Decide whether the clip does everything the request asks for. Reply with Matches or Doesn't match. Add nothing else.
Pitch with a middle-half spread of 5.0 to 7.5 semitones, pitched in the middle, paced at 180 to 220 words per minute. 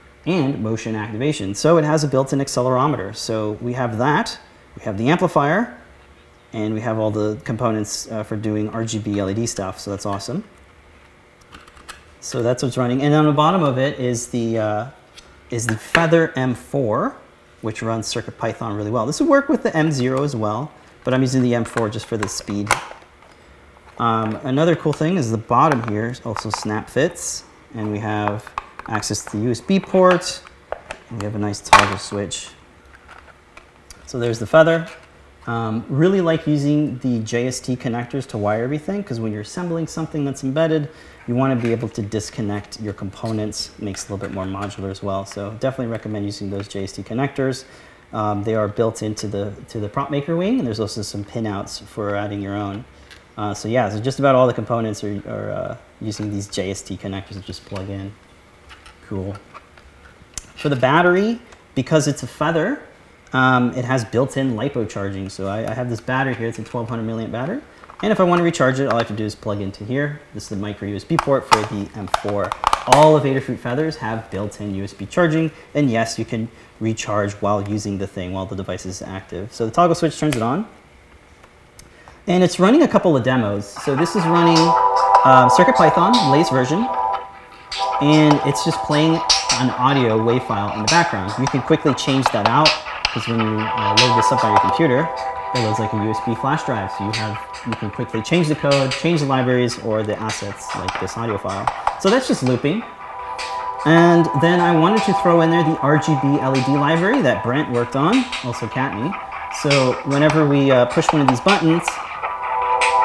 Doesn't match